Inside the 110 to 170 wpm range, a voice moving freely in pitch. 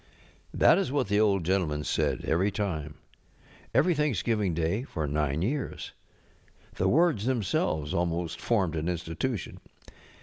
Yes: slow, 135 wpm; wide, 6.3 semitones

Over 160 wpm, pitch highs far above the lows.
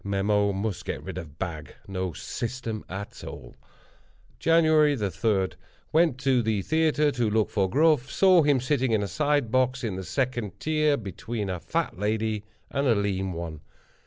No: average, 155 wpm; wide, 6.1 semitones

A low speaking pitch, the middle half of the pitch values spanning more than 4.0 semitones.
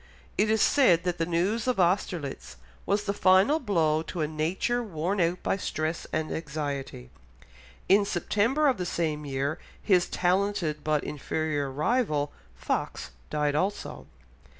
No: medium, 170 Hz; average, 4.9 semitones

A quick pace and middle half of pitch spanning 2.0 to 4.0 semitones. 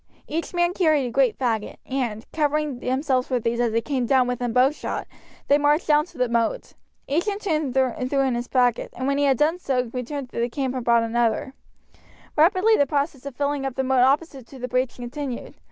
Yes: fast, 215 wpm; average, 3.2 semitones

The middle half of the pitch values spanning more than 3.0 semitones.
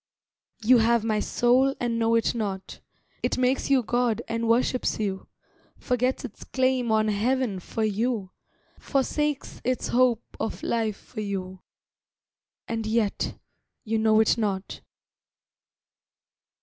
No: average, 2.7 semitones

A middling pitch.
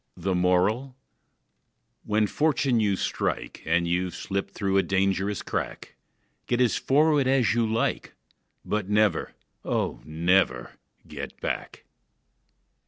No: low, 100 Hz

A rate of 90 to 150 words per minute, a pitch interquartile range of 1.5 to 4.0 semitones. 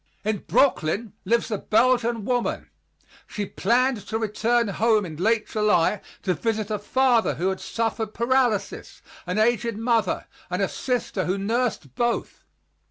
Yes: average, 145 wpm; average, 2.9 semitones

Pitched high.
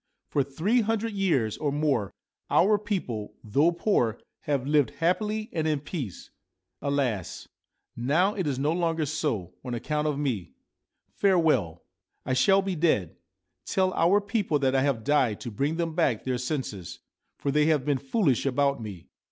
No: medium, 145 Hz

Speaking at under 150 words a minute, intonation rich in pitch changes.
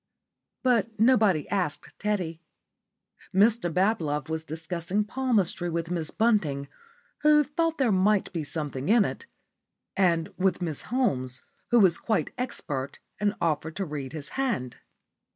Yes: slow, 135 wpm; wide, 5.9 semitones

